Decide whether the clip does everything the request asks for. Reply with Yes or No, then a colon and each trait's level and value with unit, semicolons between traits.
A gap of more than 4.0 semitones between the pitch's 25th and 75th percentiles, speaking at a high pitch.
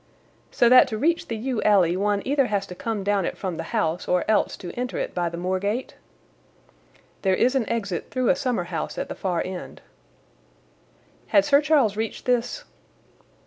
Yes: average, 5.1 semitones; high, 215 Hz